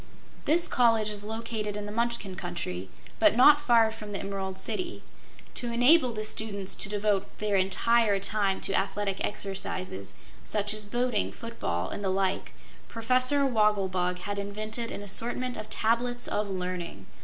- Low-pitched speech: No, high, 210 Hz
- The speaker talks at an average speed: Yes, average, 155 wpm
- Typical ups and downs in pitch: Yes, average, 3.2 semitones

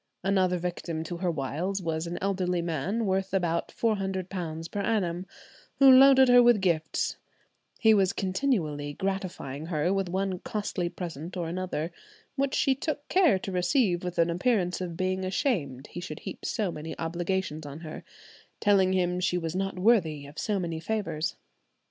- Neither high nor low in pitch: Yes, medium, 180 Hz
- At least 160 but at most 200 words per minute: Yes, average, 165 wpm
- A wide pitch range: No, average, 3.0 semitones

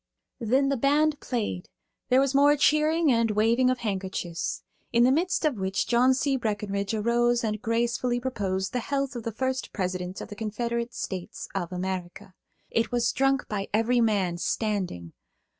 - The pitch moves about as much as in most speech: Yes, average, 4.7 semitones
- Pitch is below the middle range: No, high, 230 Hz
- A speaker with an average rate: Yes, average, 165 wpm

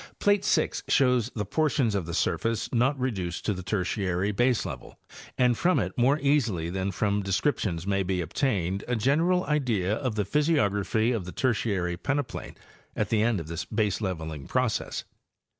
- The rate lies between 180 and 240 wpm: No, average, 165 wpm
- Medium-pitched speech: No, low, 105 Hz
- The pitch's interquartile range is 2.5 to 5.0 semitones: No, wide, 5.5 semitones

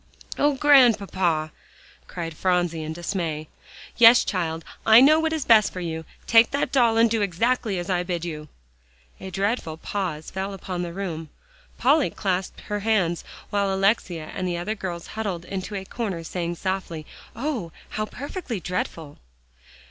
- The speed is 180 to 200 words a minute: No, average, 155 wpm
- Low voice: No, high, 190 Hz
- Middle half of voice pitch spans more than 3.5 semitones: Yes, average, 4.6 semitones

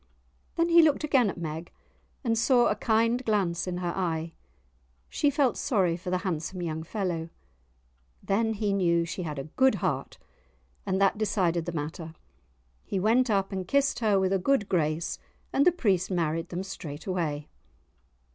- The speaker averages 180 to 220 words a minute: No, average, 170 wpm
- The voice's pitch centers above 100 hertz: Yes, high, 190 Hz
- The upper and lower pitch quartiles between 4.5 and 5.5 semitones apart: Yes, average, 4.8 semitones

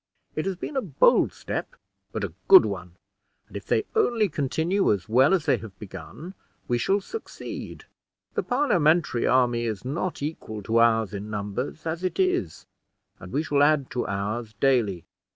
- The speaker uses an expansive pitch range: Yes, wide, 7.9 semitones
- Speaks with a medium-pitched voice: No, low, 130 Hz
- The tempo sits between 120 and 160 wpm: No, average, 170 wpm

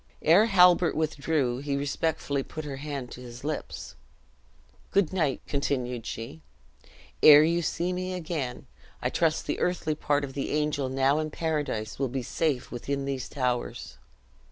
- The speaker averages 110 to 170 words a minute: Yes, average, 155 wpm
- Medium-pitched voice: Yes, medium, 145 Hz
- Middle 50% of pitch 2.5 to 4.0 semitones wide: Yes, average, 3.2 semitones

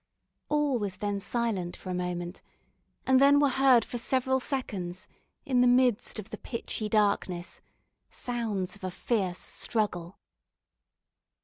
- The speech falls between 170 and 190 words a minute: No, slow, 135 wpm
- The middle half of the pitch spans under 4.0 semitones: No, wide, 5.4 semitones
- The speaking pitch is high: Yes, high, 215 Hz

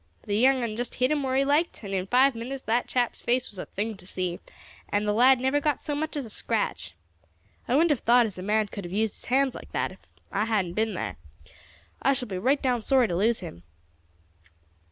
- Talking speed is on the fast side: Yes, fast, 235 wpm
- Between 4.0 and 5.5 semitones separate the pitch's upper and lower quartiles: Yes, average, 4.4 semitones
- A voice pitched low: No, high, 235 Hz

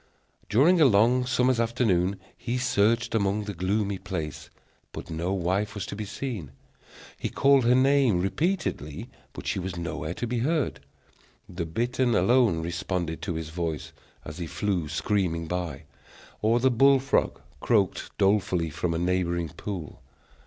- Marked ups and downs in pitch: Yes, wide, 5.9 semitones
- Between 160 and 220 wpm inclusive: No, average, 150 wpm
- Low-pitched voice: Yes, low, 100 Hz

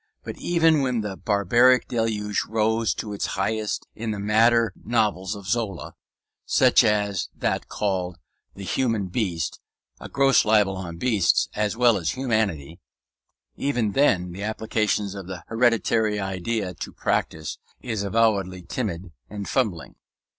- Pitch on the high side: No, low, 105 Hz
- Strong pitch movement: No, average, 3.1 semitones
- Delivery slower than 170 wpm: Yes, average, 140 wpm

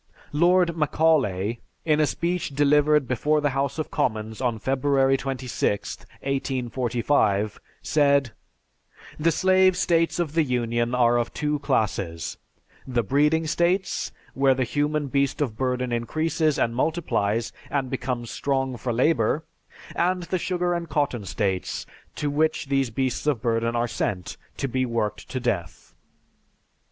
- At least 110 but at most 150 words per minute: Yes, average, 140 wpm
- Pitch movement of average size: Yes, average, 4.3 semitones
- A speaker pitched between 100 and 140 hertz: Yes, low, 135 Hz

